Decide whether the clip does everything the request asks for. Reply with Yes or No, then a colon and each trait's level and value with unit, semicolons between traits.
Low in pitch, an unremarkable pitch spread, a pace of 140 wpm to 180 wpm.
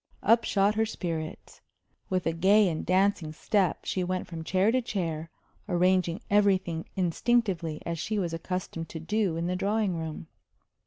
No: medium, 185 Hz; average, 3.4 semitones; average, 160 wpm